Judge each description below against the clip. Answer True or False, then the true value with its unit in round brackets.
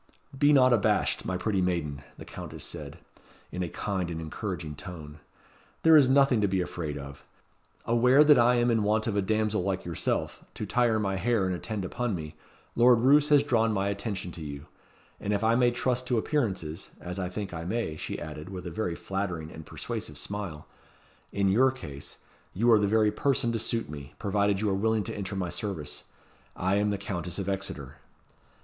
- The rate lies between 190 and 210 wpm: True (200 wpm)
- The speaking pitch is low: True (100 Hz)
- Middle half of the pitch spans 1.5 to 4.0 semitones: False (4.8 semitones)